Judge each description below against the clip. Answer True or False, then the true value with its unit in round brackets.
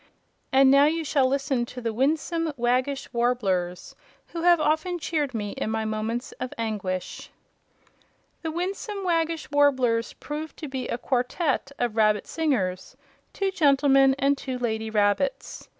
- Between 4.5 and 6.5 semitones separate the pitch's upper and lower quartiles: True (5.1 semitones)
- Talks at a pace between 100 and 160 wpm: True (145 wpm)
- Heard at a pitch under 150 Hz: False (265 Hz)